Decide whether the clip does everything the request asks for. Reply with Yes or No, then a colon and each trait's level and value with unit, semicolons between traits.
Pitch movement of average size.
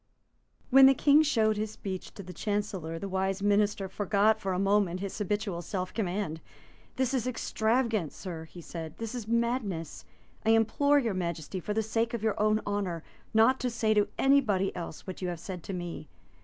Yes: average, 3.4 semitones